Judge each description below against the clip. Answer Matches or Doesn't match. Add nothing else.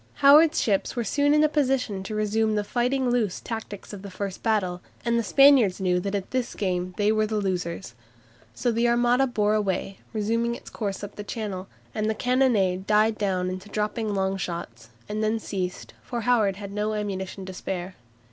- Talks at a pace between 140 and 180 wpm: Doesn't match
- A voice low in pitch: Doesn't match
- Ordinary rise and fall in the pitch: Matches